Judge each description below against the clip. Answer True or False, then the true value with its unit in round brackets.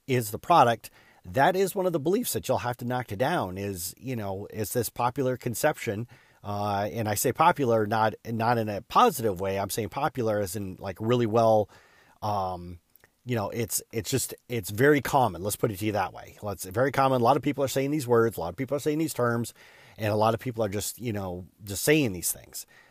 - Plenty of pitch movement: False (3.7 semitones)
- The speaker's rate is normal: False (240 wpm)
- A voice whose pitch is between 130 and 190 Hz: False (115 Hz)